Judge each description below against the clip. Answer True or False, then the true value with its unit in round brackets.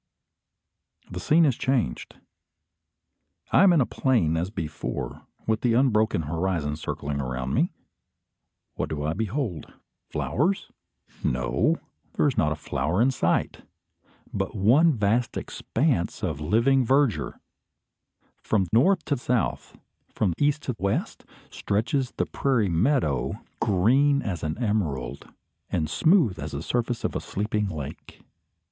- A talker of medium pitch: False (110 Hz)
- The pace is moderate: False (130 wpm)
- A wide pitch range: True (8.6 semitones)